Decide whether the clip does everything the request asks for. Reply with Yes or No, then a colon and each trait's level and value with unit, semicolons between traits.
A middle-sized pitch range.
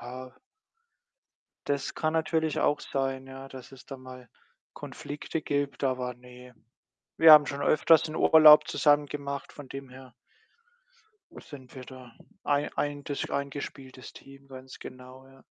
No: narrow, 2.0 semitones